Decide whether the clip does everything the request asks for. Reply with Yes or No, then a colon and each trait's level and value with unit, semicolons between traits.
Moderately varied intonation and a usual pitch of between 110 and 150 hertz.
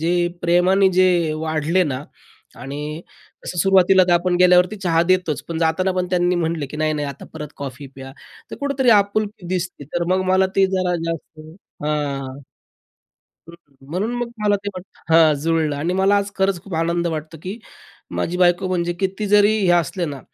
No: average, 3.3 semitones; medium, 175 Hz